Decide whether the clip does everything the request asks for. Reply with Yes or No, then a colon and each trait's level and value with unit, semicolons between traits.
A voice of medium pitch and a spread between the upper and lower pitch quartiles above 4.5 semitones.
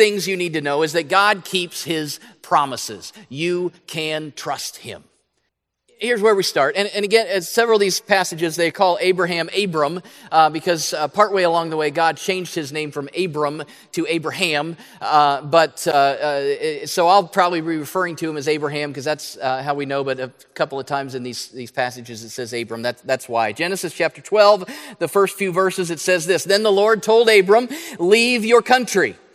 Yes: medium, 170 Hz; average, 5.0 semitones